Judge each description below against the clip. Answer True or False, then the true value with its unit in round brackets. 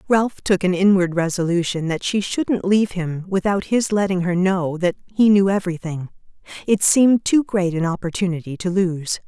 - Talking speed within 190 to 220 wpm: False (175 wpm)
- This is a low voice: False (185 Hz)